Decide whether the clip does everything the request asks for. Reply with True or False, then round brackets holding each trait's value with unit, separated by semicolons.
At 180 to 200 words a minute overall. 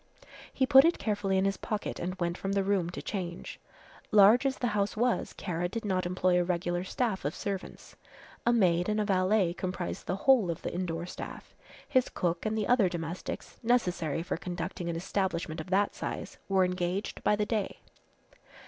True (190 wpm)